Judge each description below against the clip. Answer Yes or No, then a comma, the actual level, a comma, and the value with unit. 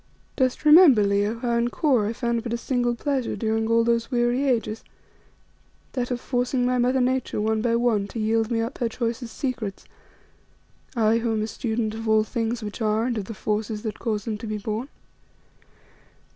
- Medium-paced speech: Yes, average, 195 wpm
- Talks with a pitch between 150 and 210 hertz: No, high, 230 Hz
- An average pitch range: No, narrow, 2.1 semitones